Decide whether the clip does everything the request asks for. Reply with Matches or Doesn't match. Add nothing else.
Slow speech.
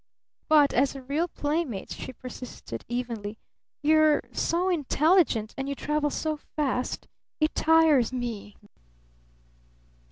Matches